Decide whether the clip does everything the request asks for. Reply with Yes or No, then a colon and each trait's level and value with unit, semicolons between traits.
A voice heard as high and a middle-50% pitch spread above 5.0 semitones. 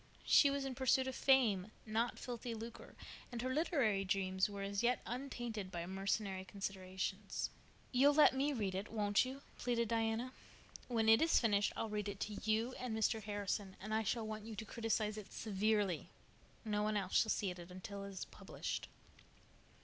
No: high, 215 Hz; average, 3.3 semitones